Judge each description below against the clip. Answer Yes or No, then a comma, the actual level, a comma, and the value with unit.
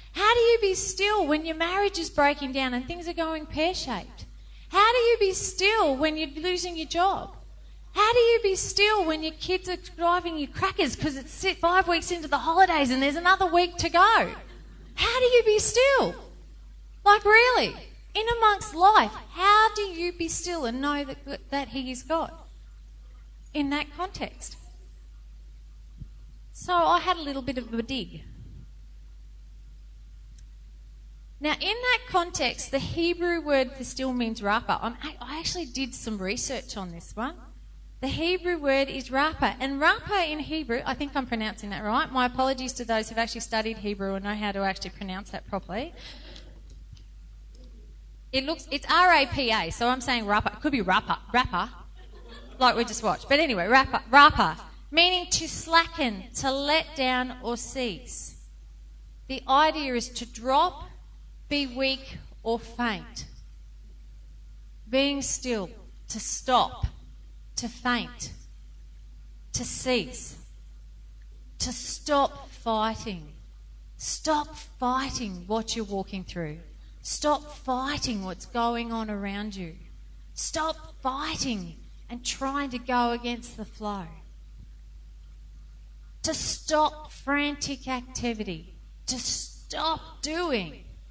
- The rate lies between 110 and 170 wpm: Yes, average, 140 wpm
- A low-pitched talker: No, very high, 265 Hz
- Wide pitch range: Yes, wide, 7.4 semitones